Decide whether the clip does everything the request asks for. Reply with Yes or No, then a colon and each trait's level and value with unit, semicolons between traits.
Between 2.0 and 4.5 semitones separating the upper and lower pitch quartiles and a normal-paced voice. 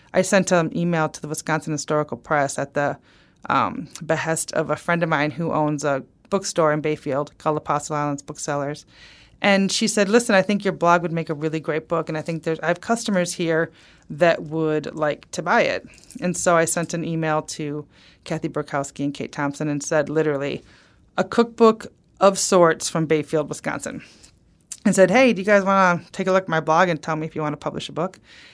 No: average, 3.0 semitones; fast, 215 wpm